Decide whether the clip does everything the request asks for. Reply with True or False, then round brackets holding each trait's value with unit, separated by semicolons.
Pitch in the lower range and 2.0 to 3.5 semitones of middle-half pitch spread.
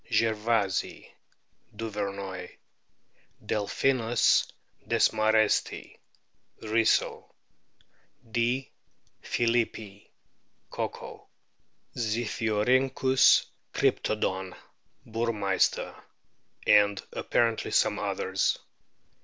True (110 Hz; 2.4 semitones)